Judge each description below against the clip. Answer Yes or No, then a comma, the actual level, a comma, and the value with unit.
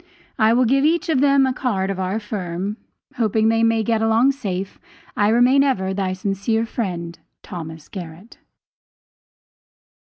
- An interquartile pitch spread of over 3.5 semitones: Yes, average, 4.2 semitones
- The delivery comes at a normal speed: Yes, average, 155 wpm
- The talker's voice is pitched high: Yes, high, 220 Hz